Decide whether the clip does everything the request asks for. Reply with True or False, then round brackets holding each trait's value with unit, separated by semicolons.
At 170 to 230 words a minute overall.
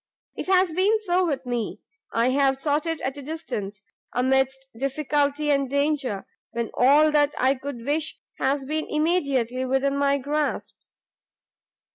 False (145 wpm)